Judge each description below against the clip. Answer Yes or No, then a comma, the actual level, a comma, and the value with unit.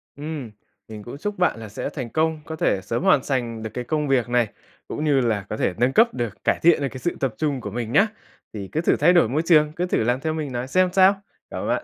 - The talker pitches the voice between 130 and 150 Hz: Yes, low, 135 Hz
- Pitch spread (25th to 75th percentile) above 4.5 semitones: Yes, average, 5.2 semitones